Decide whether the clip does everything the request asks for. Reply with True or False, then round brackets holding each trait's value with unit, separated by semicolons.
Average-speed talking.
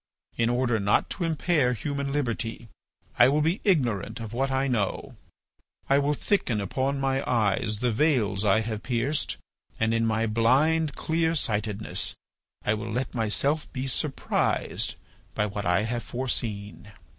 True (145 wpm)